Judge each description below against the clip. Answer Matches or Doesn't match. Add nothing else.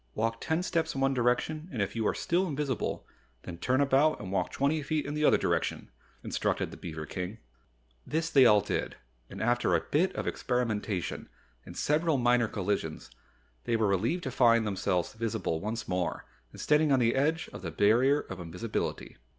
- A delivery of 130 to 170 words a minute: Doesn't match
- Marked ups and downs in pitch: Matches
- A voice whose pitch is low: Matches